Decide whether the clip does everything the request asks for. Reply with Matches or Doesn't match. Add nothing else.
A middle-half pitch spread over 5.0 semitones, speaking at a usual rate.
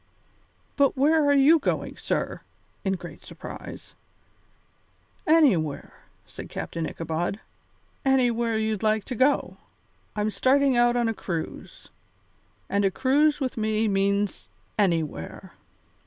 Doesn't match